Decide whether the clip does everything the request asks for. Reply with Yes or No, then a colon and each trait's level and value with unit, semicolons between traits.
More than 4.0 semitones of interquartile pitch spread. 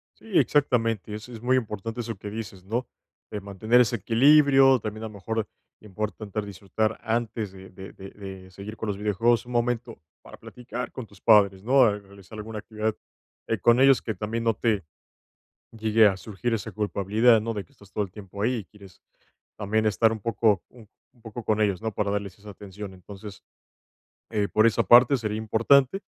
No: narrow, 2.4 semitones